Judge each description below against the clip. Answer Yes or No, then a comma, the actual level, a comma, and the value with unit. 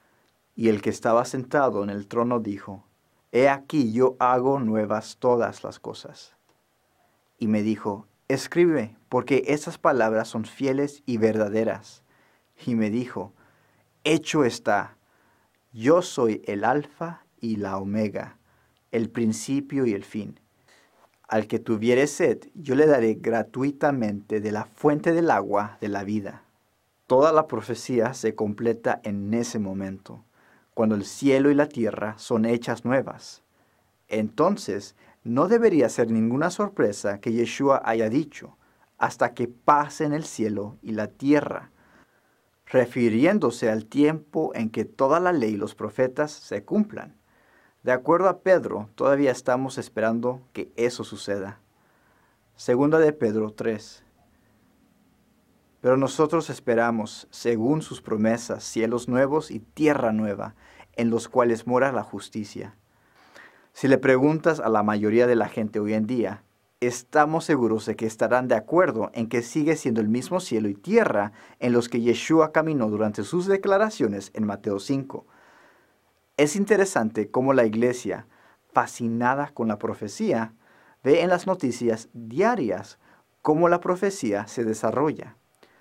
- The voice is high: No, low, 120 Hz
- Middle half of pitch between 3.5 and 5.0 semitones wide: Yes, average, 4.4 semitones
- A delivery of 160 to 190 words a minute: No, average, 140 wpm